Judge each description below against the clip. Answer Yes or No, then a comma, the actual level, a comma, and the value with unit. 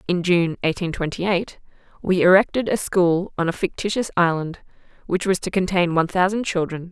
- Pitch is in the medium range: Yes, medium, 180 Hz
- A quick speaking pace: No, average, 175 wpm